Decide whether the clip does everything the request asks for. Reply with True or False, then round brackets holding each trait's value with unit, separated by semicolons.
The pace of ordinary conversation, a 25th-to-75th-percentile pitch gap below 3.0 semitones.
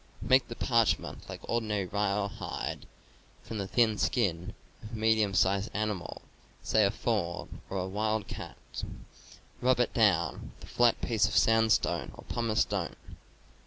True (145 wpm; 2.5 semitones)